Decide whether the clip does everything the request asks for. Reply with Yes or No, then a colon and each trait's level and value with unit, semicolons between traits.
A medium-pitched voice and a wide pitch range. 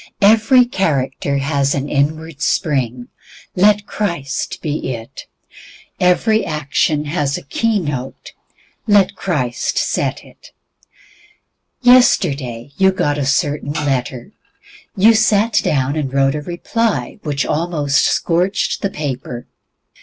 Yes: medium, 150 Hz; wide, 5.9 semitones